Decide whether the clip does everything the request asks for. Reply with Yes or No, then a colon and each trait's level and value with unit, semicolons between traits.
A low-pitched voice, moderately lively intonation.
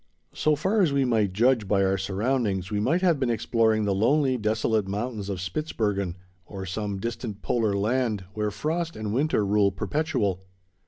Yes: low, 110 Hz; average, 4.7 semitones